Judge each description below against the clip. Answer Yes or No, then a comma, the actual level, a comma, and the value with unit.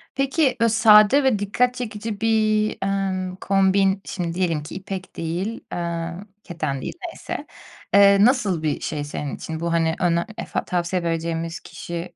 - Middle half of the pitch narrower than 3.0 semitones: No, average, 4.1 semitones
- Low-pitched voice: No, high, 190 Hz